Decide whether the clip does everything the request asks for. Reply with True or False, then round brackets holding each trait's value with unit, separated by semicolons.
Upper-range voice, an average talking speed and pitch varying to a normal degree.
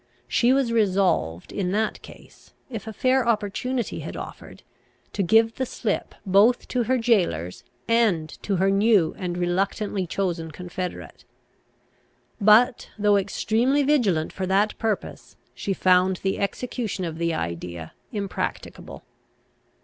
False (200 Hz; 130 wpm; 4.0 semitones)